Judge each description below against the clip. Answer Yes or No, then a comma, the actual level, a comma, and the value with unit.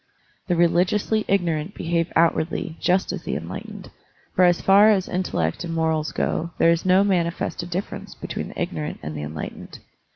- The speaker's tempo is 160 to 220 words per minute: Yes, average, 170 wpm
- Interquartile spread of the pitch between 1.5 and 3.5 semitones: Yes, narrow, 2.5 semitones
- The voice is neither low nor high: Yes, medium, 170 Hz